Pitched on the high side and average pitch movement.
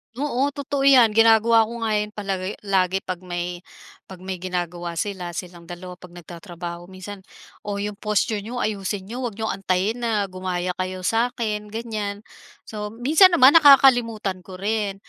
Yes: high, 205 Hz; average, 3.6 semitones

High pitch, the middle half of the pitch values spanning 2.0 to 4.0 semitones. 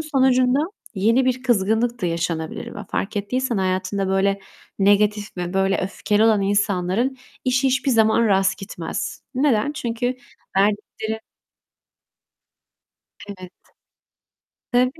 No: high, 210 Hz; average, 4.5 semitones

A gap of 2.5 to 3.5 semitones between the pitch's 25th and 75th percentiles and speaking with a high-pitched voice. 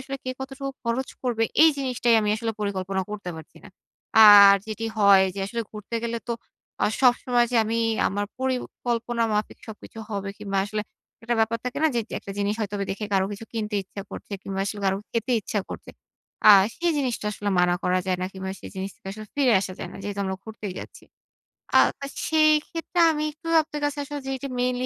No: average, 4.1 semitones; high, 220 Hz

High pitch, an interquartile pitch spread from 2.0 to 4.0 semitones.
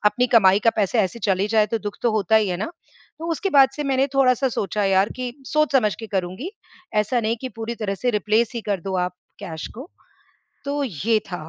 No: high, 220 Hz; average, 4.6 semitones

